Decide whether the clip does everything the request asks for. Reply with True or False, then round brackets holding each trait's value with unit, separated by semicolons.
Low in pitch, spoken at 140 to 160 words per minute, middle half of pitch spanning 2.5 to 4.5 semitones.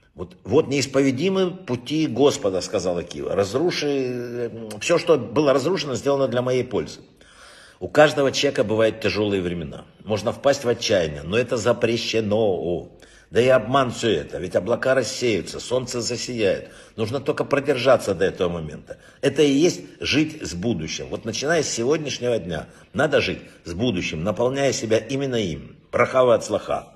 True (125 Hz; 150 wpm; 4.0 semitones)